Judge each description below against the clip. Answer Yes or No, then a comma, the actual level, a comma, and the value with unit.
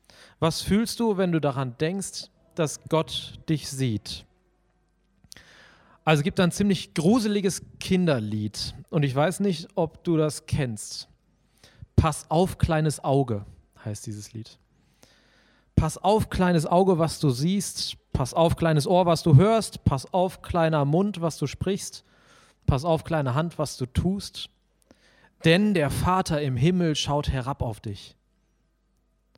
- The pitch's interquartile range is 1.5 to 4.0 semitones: No, average, 5.1 semitones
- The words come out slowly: No, average, 145 wpm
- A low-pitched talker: No, medium, 155 Hz